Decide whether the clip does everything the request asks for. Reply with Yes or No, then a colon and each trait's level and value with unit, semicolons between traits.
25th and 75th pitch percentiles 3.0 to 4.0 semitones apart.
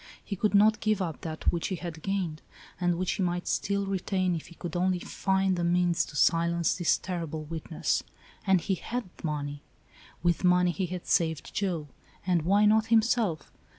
No: narrow, 2.6 semitones